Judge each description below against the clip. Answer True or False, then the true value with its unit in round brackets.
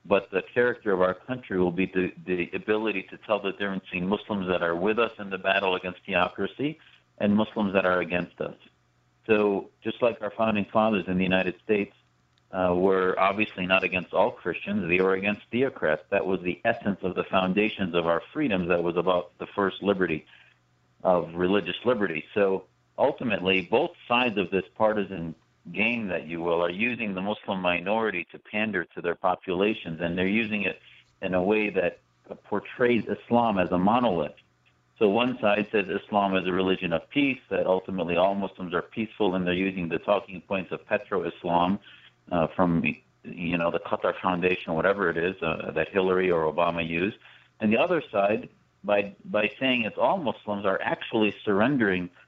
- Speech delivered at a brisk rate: False (185 wpm)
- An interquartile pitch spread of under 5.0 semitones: True (2.8 semitones)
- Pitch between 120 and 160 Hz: False (95 Hz)